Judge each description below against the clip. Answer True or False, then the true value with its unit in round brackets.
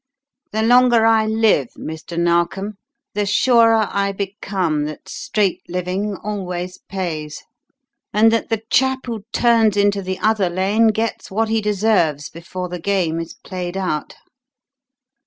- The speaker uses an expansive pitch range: False (3.7 semitones)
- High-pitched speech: True (200 Hz)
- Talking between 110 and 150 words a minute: True (140 wpm)